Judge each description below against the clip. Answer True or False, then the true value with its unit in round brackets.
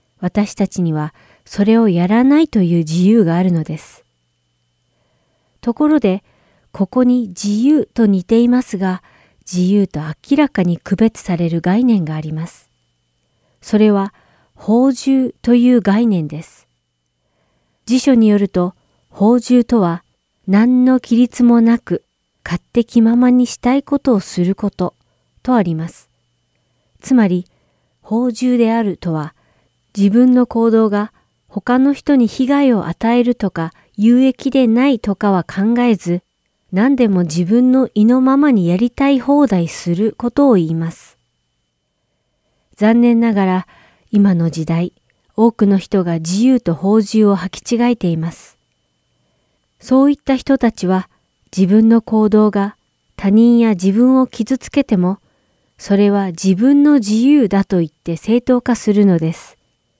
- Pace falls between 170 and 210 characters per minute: False (250 characters per minute)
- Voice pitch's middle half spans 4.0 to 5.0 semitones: False (5.6 semitones)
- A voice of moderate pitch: False (210 Hz)